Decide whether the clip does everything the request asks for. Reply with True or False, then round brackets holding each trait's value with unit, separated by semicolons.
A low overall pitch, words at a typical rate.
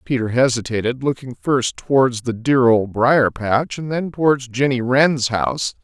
True (125 Hz; 165 wpm)